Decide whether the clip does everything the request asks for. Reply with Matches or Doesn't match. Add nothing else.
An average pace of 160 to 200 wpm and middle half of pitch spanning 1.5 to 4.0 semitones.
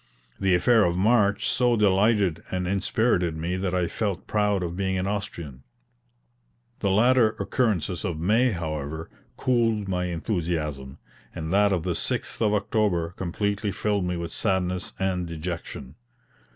Doesn't match